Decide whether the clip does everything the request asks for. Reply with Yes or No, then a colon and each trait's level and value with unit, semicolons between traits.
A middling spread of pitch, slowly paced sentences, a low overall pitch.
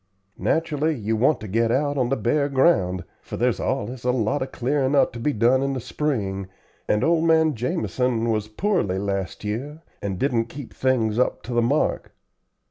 No: average, 4.9 semitones; average, 190 wpm; low, 125 Hz